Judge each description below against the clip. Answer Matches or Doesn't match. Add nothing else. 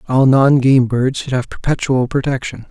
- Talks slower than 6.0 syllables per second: Matches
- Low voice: Matches